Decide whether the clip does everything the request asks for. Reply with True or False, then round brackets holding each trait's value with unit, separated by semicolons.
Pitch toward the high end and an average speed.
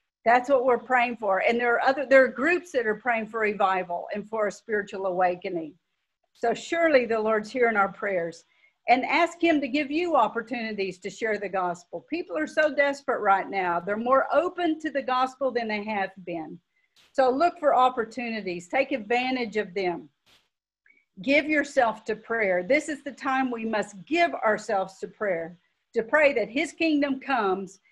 True (230 Hz; 180 wpm)